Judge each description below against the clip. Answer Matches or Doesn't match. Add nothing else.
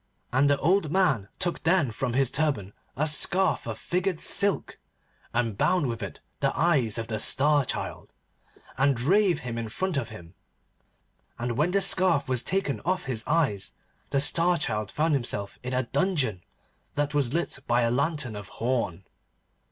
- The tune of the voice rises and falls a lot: Matches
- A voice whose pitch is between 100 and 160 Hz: Matches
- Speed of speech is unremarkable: Matches